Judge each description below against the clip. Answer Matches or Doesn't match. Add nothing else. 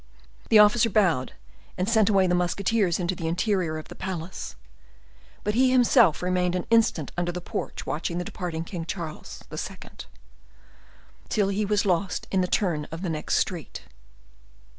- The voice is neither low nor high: Matches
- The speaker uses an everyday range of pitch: Matches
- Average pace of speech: Matches